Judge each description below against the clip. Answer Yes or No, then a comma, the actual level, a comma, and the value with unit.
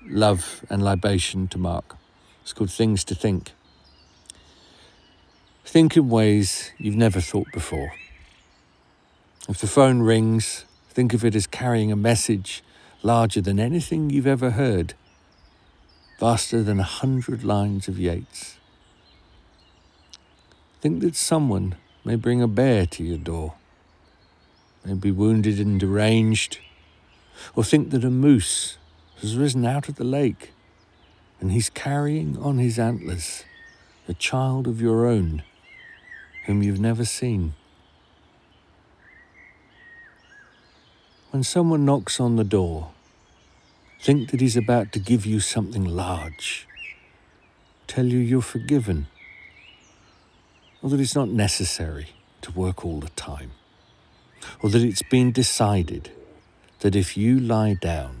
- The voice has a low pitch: Yes, low, 100 Hz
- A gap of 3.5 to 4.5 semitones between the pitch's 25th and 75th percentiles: No, wide, 5.5 semitones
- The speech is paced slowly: Yes, slow, 125 wpm